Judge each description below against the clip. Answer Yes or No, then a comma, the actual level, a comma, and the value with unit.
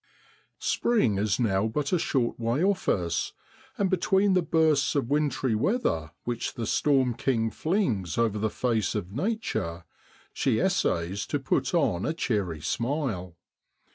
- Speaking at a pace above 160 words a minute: No, average, 145 wpm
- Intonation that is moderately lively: No, wide, 7.3 semitones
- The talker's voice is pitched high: No, low, 120 Hz